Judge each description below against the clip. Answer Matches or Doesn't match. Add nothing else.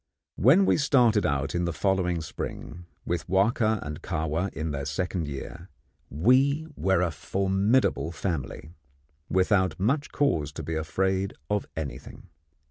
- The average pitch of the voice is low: Matches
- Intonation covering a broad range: Doesn't match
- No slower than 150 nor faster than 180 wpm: Doesn't match